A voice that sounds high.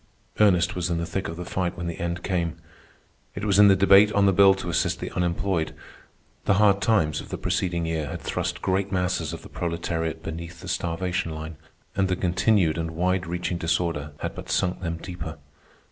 No: very low, 90 Hz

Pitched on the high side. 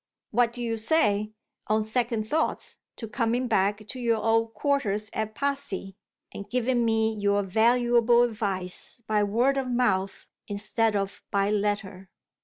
Yes: high, 220 Hz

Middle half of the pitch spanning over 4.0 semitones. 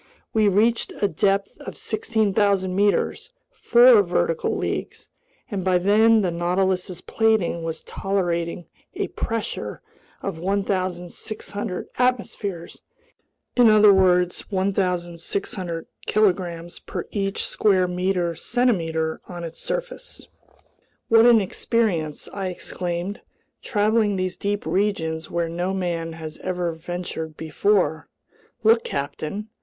No: average, 3.5 semitones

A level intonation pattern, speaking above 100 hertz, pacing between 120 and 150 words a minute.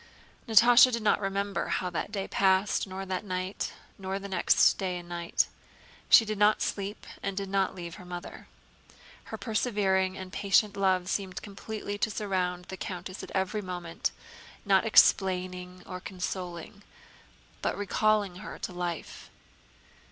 Yes: narrow, 1.9 semitones; high, 190 Hz; average, 145 wpm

